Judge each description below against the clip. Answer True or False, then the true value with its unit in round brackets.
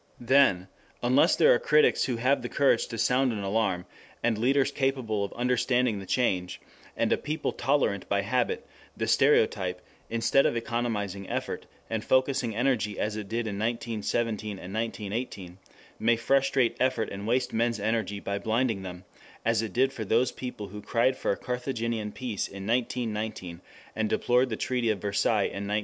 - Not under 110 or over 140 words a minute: False (170 wpm)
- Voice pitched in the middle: False (115 Hz)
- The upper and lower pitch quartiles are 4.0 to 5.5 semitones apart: False (3.4 semitones)